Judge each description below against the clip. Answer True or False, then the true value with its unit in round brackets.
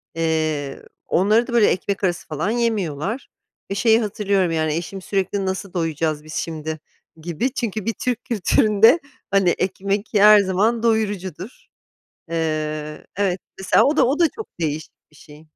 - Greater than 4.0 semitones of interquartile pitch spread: True (5.2 semitones)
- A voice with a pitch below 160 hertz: False (190 Hz)